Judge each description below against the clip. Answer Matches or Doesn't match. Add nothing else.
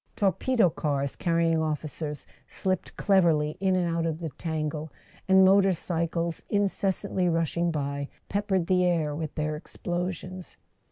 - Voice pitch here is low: Doesn't match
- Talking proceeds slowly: Matches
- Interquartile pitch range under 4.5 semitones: Matches